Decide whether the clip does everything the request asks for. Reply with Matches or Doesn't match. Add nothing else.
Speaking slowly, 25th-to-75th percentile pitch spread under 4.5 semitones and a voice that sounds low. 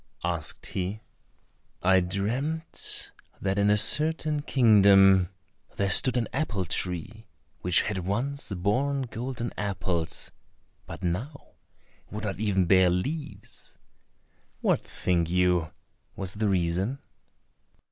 Doesn't match